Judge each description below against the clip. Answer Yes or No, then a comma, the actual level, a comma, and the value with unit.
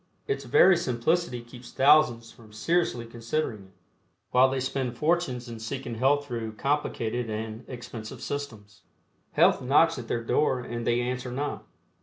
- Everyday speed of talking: Yes, average, 150 wpm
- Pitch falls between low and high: No, low, 125 Hz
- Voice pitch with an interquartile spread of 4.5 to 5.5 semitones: No, average, 3.5 semitones